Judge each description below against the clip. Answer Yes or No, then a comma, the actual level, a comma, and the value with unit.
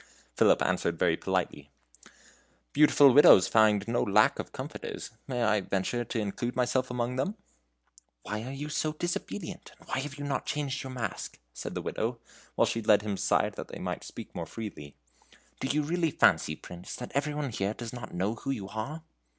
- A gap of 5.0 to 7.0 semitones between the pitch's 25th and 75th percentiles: Yes, average, 5.3 semitones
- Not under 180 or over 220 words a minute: Yes, average, 190 wpm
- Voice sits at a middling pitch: No, low, 120 Hz